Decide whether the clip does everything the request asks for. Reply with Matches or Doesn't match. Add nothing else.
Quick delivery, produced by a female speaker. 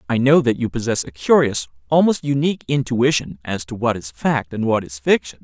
Doesn't match